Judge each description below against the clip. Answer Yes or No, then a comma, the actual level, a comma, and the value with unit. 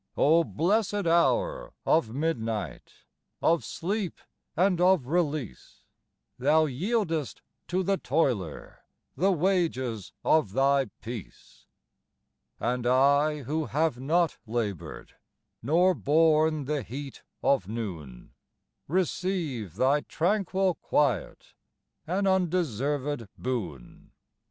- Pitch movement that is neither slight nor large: No, wide, 6.1 semitones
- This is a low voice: No, medium, 150 Hz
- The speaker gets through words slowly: Yes, slow, 95 wpm